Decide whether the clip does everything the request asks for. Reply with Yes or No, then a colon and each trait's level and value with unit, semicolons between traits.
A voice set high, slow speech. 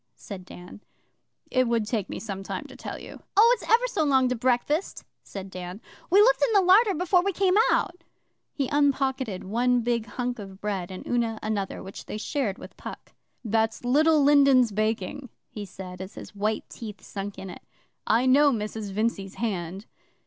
No: high, 230 Hz; average, 185 wpm